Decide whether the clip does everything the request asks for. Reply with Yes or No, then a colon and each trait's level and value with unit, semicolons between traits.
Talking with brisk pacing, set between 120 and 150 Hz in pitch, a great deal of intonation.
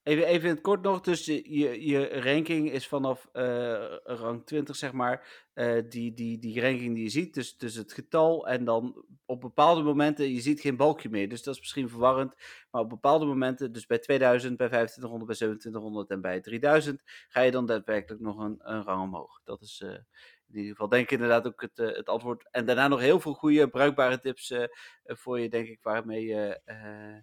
No: fast, 215 wpm; low, 125 Hz; average, 3.7 semitones